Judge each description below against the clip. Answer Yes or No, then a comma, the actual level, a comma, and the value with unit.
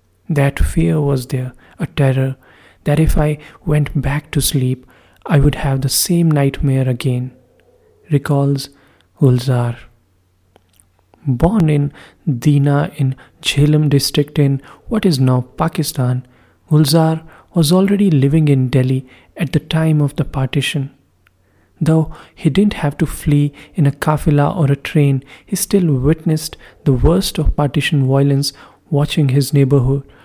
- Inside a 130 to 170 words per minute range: Yes, slow, 135 wpm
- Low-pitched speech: No, medium, 145 Hz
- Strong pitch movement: No, average, 2.7 semitones